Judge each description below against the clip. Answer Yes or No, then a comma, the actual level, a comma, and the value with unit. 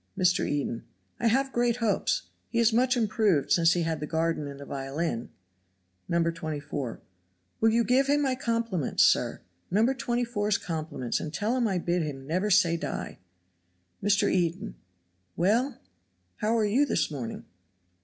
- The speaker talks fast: No, average, 155 wpm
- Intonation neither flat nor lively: No, wide, 6.7 semitones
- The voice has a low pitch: No, medium, 185 Hz